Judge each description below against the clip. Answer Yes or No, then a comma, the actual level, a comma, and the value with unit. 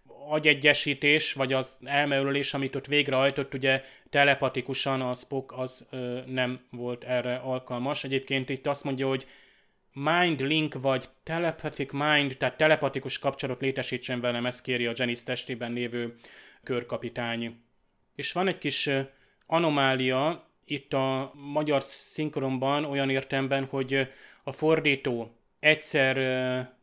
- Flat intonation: Yes, narrow, 1.9 semitones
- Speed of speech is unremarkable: Yes, average, 125 wpm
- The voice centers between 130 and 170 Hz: Yes, low, 135 Hz